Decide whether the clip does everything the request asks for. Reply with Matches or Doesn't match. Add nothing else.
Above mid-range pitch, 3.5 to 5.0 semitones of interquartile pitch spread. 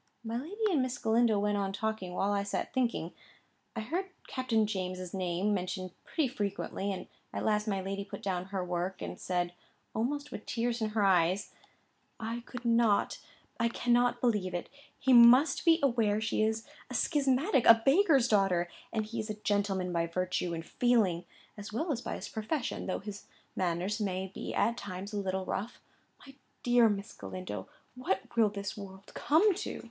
Matches